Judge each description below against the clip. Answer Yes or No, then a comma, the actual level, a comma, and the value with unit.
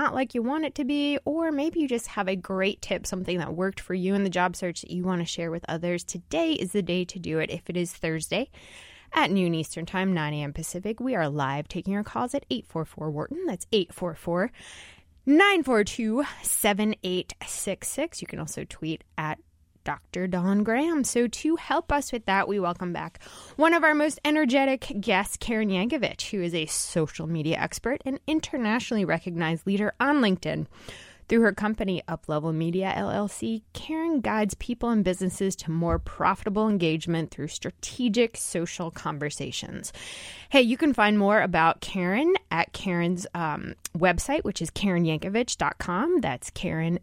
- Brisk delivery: No, average, 165 wpm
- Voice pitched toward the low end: No, high, 190 Hz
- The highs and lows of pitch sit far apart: Yes, wide, 6.4 semitones